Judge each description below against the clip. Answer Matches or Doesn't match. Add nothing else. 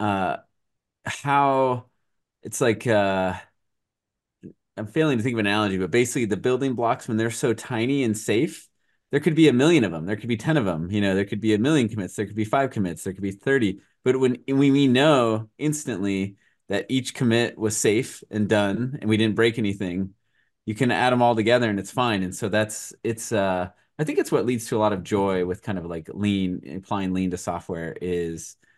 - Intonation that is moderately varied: Matches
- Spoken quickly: Matches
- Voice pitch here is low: Matches